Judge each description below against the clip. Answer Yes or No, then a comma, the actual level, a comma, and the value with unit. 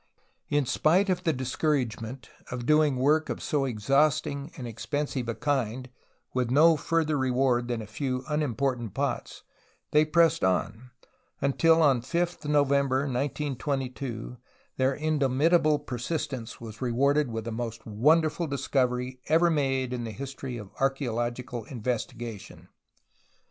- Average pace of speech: No, slow, 130 wpm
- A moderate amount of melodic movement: Yes, average, 3.7 semitones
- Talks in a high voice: No, low, 135 Hz